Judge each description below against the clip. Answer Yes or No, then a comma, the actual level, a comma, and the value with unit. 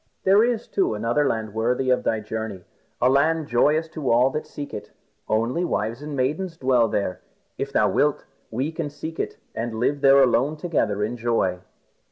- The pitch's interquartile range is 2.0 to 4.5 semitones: No, average, 5.2 semitones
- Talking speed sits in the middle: Yes, average, 185 wpm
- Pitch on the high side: No, low, 130 Hz